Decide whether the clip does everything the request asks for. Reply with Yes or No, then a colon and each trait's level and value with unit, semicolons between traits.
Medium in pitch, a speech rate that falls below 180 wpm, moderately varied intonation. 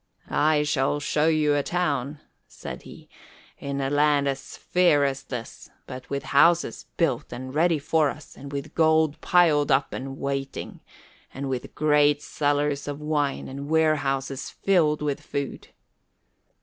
No: medium, 145 Hz; average, 150 wpm; narrow, 1.9 semitones